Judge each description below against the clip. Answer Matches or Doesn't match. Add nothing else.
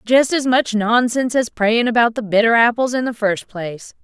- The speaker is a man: Doesn't match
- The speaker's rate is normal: Doesn't match